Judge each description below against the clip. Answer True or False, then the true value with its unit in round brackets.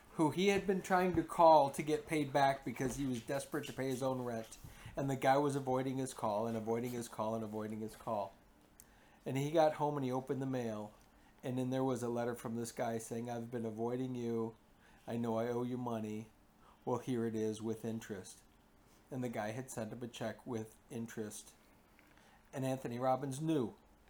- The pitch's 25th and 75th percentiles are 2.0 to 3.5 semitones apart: True (3.2 semitones)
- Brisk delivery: True (210 wpm)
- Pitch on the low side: True (120 Hz)